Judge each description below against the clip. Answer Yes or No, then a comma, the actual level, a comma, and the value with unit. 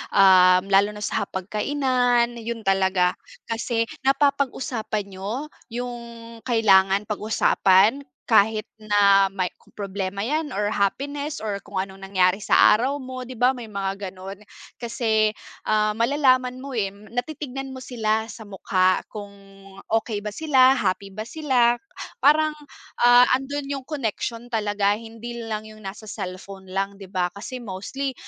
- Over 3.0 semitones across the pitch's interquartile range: Yes, average, 4.1 semitones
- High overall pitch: Yes, high, 220 Hz